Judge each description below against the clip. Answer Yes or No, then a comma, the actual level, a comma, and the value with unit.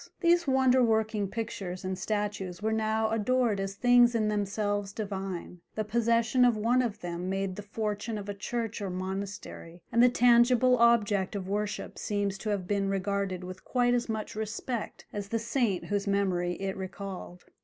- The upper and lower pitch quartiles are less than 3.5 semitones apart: Yes, average, 2.9 semitones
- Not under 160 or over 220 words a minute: Yes, average, 175 wpm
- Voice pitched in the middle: No, high, 210 Hz